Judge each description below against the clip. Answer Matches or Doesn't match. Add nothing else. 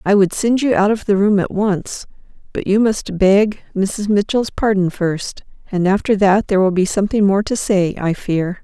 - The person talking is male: Doesn't match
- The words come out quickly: Matches